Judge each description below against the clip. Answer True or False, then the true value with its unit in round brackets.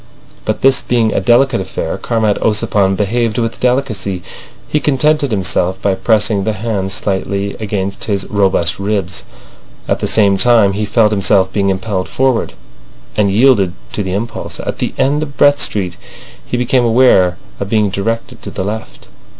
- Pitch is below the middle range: True (105 Hz)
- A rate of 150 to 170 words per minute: True (165 wpm)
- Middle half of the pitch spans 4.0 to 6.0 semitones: False (3.4 semitones)